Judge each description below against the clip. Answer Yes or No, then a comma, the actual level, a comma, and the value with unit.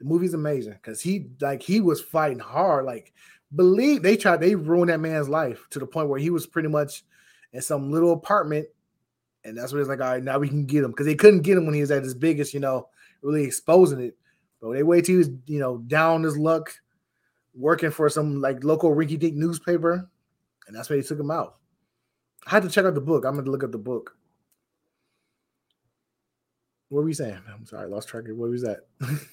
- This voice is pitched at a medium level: Yes, medium, 150 Hz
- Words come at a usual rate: No, fast, 225 wpm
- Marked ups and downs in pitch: No, average, 3.7 semitones